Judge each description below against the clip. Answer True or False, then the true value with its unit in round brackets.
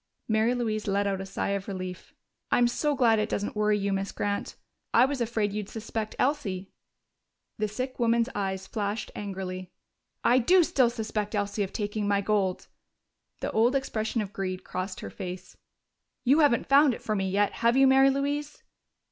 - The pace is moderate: True (180 wpm)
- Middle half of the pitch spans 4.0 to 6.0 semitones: False (3.4 semitones)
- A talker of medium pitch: False (215 Hz)